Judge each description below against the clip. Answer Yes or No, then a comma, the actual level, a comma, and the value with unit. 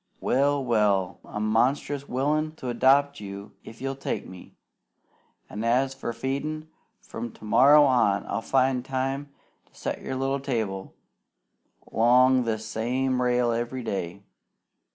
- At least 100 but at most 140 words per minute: Yes, slow, 135 wpm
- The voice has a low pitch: Yes, low, 125 Hz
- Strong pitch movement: No, average, 3.5 semitones